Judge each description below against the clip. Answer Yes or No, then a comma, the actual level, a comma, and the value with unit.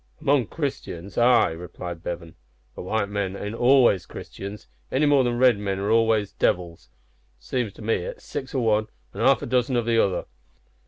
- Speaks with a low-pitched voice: Yes, low, 110 Hz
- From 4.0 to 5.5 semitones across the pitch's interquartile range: Yes, average, 4.4 semitones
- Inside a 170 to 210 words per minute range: Yes, average, 180 wpm